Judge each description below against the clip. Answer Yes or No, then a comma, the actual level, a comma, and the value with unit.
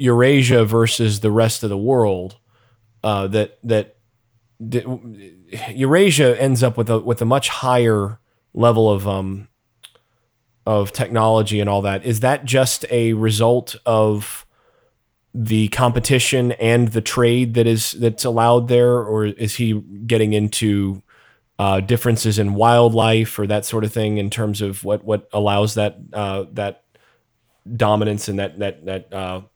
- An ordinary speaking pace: Yes, average, 150 wpm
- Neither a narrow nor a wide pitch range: No, narrow, 2.3 semitones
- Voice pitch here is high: No, low, 110 Hz